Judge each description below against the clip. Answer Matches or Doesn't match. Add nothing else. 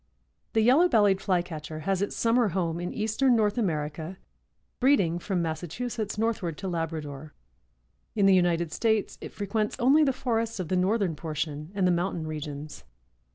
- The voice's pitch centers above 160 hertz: Matches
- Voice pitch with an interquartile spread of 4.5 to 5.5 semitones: Matches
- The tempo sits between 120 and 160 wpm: Matches